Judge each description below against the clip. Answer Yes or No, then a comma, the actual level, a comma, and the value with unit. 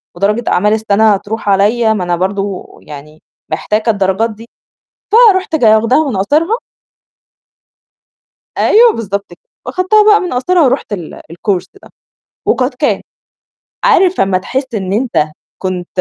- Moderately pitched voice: No, high, 215 Hz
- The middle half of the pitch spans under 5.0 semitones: No, wide, 5.6 semitones